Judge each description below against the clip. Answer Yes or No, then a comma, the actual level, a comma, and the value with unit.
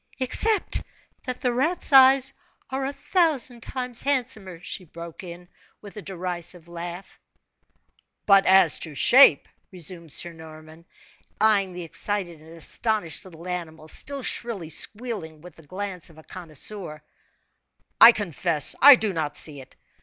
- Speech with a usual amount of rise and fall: No, wide, 6.2 semitones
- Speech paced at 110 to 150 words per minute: Yes, average, 140 wpm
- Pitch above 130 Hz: Yes, medium, 185 Hz